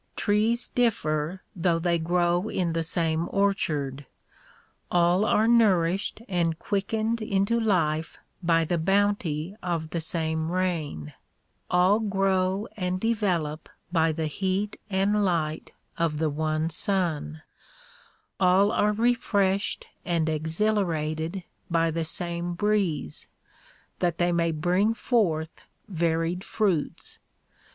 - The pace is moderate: No, slow, 110 wpm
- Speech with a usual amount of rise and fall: Yes, average, 3.7 semitones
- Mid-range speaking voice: Yes, medium, 175 Hz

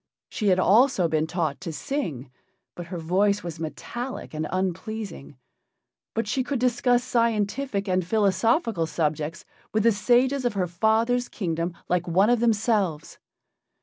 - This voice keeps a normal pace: Yes, average, 145 wpm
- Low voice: No, high, 200 Hz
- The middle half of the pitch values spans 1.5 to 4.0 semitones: No, wide, 5.5 semitones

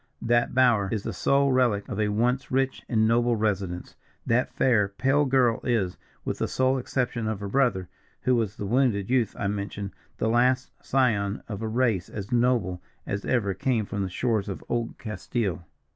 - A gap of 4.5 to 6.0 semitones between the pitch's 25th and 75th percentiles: No, average, 3.8 semitones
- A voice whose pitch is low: Yes, low, 115 Hz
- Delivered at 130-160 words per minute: No, average, 185 wpm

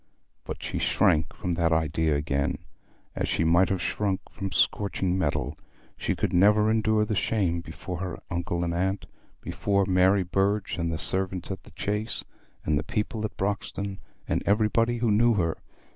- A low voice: Yes, very low, 95 Hz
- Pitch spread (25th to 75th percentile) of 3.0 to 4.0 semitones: Yes, average, 3.5 semitones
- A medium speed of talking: Yes, average, 170 wpm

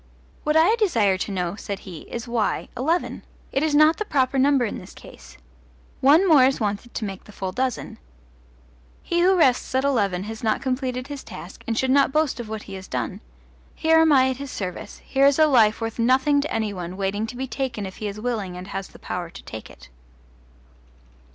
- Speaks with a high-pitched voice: Yes, high, 245 Hz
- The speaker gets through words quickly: Yes, fast, 215 wpm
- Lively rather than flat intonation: Yes, wide, 5.7 semitones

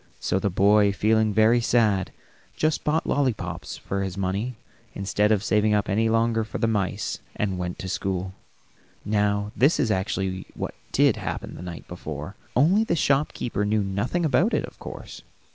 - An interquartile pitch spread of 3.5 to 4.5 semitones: No, average, 3.0 semitones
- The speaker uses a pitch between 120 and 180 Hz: No, low, 105 Hz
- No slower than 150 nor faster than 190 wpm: Yes, average, 170 wpm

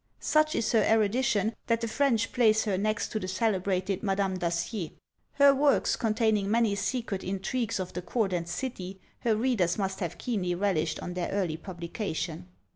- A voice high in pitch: Yes, high, 200 Hz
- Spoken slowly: No, average, 170 wpm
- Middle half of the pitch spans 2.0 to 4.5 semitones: Yes, average, 3.7 semitones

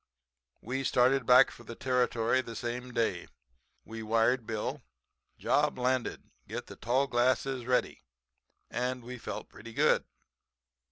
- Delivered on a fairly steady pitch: Yes, narrow, 1.6 semitones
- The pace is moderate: No, slow, 130 wpm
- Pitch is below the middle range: Yes, low, 125 Hz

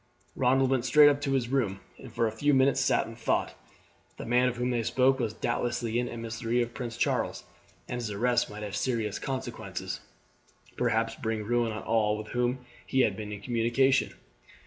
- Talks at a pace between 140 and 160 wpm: No, average, 190 wpm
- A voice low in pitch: Yes, low, 120 Hz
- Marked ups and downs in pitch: No, narrow, 2.5 semitones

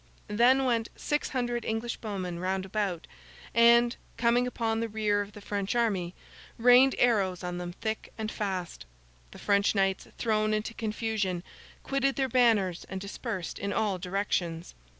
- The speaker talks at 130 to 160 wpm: Yes, average, 150 wpm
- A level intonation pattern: No, average, 3.6 semitones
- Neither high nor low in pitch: No, high, 215 Hz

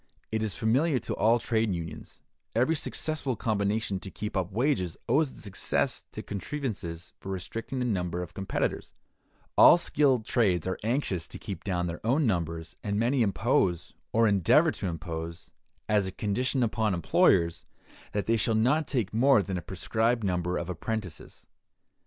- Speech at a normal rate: Yes, average, 165 wpm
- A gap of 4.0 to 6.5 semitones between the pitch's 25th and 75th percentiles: Yes, average, 5.0 semitones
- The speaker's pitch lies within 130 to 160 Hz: No, low, 105 Hz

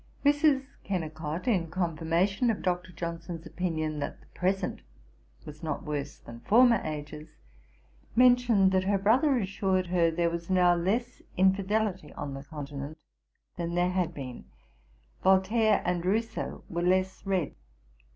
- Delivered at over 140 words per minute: No, slow, 135 wpm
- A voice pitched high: No, medium, 180 Hz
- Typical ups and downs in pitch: Yes, average, 3.7 semitones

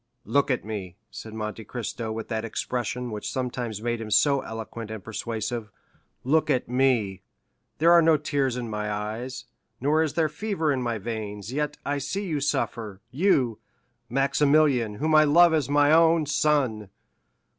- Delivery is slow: No, average, 155 wpm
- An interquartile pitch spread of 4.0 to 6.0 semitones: Yes, average, 5.1 semitones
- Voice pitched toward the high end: No, low, 125 Hz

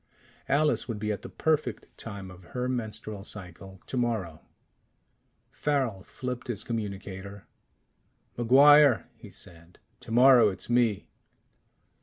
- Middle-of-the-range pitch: No, low, 110 Hz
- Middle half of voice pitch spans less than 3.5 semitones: No, average, 4.3 semitones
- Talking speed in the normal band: No, slow, 110 wpm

